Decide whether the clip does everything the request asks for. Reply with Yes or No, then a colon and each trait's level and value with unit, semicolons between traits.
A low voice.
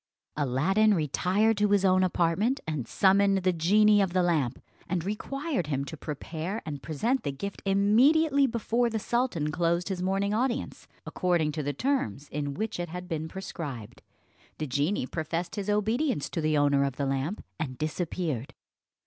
No: medium, 180 Hz